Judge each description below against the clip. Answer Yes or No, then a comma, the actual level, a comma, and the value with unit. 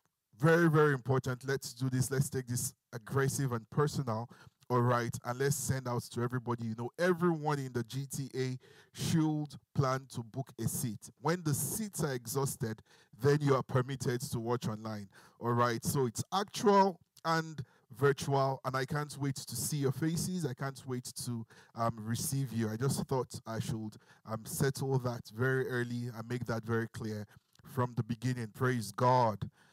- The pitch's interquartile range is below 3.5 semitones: Yes, average, 2.9 semitones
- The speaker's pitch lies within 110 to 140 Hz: Yes, low, 130 Hz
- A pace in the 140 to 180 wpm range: Yes, average, 175 wpm